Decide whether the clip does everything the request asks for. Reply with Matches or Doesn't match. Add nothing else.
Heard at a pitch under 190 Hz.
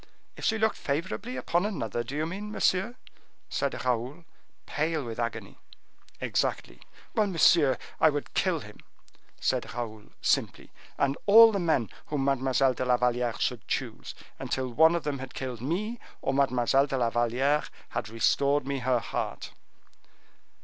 Matches